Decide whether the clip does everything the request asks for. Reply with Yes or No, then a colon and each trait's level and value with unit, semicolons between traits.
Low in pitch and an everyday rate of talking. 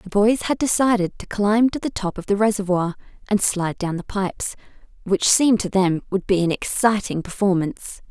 No: high, 200 Hz; average, 190 wpm